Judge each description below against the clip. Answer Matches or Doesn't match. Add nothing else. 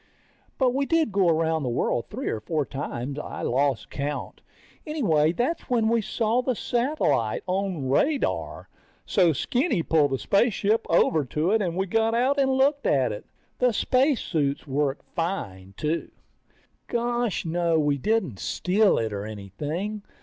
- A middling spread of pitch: Doesn't match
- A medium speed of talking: Matches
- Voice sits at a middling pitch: Matches